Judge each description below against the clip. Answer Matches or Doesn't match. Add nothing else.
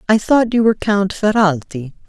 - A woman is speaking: Matches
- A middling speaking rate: Matches